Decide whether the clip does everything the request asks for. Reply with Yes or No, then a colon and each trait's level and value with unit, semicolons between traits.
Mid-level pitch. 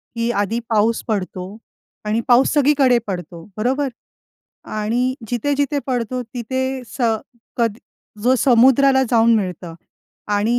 No: high, 235 Hz